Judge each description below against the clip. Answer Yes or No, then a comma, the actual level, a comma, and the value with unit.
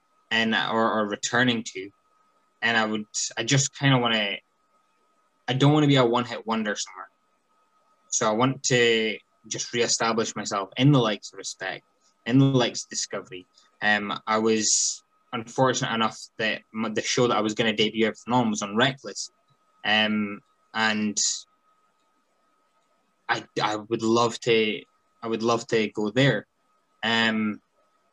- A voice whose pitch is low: Yes, low, 115 Hz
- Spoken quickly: No, average, 160 wpm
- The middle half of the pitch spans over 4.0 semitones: Yes, average, 4.6 semitones